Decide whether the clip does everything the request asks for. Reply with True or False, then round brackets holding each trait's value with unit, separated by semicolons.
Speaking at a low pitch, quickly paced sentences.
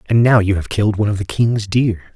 True (105 Hz; 280 wpm)